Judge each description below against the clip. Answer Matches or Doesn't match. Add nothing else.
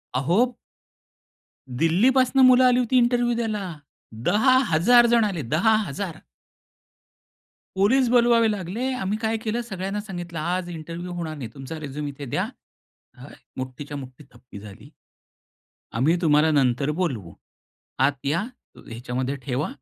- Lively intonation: Matches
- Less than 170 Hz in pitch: Doesn't match